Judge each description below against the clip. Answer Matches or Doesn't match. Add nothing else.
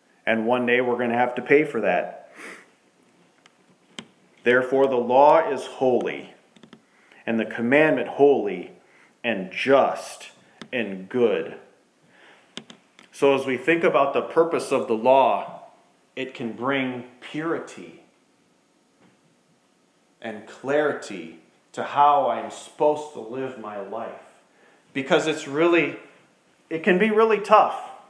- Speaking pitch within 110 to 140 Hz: Matches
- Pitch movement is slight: Doesn't match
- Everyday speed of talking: Doesn't match